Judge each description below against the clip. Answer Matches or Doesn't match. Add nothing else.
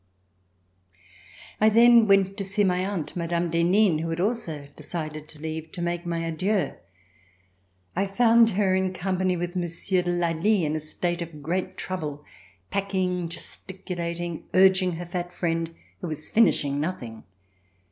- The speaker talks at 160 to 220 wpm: Doesn't match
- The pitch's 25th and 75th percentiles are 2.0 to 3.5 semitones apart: Matches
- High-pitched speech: Doesn't match